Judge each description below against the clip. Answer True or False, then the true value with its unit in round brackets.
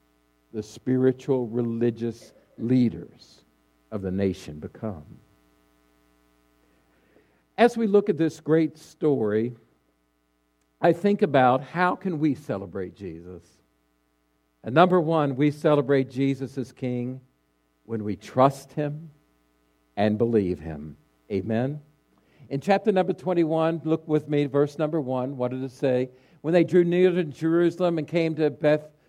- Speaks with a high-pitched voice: False (130 Hz)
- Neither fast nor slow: False (130 wpm)